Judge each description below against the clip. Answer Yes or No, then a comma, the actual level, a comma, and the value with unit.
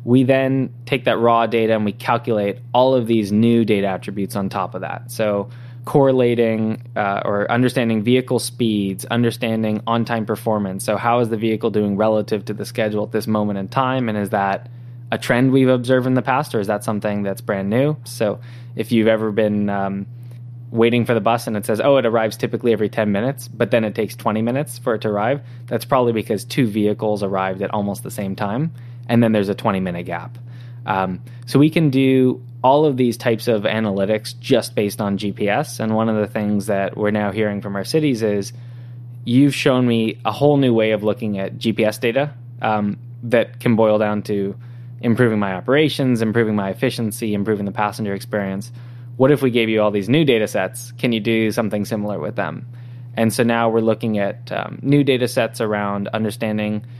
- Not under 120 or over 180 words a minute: No, fast, 205 wpm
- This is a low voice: Yes, low, 115 Hz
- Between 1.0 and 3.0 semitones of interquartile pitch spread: Yes, narrow, 2.4 semitones